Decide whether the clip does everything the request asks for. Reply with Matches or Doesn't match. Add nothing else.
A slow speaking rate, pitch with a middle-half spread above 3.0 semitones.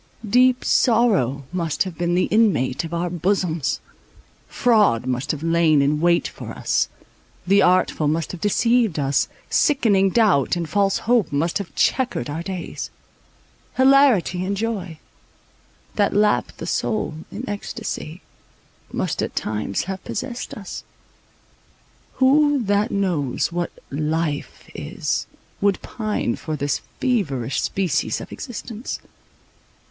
Matches